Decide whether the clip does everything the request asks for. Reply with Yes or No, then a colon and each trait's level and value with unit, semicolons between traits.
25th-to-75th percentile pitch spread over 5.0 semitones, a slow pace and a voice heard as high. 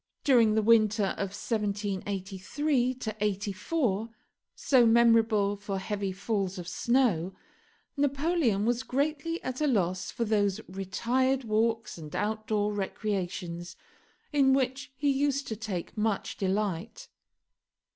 No: average, 4.4 semitones; slow, 115 wpm; high, 215 Hz